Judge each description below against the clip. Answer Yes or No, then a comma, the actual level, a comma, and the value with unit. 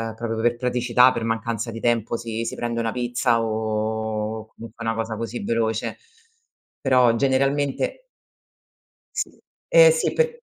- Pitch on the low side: Yes, low, 115 Hz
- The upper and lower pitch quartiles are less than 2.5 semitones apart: Yes, narrow, 2.0 semitones